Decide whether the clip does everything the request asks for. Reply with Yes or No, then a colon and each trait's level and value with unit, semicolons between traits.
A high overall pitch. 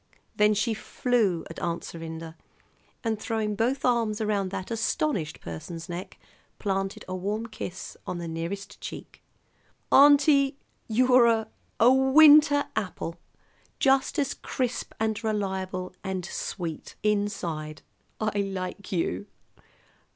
Yes: high, 210 Hz